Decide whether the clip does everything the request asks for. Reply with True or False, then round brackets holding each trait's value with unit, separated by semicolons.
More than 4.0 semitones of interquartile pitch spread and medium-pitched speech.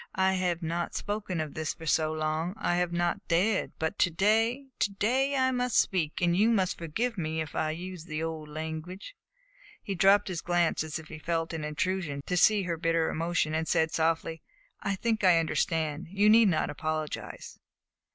False (3.5 semitones; 170 Hz)